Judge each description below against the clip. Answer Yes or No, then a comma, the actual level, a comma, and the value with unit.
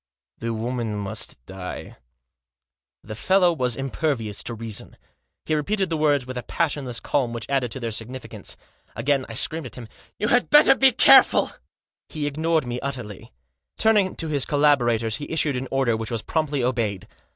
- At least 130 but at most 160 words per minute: No, average, 180 wpm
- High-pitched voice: No, low, 130 Hz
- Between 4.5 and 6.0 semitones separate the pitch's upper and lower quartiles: Yes, average, 5.1 semitones